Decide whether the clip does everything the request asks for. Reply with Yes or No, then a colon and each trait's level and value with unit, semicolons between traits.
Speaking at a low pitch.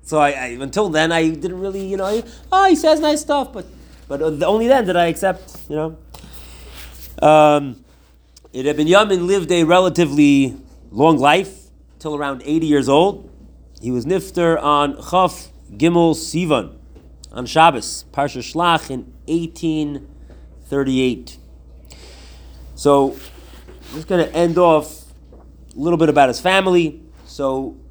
No: medium, 150 Hz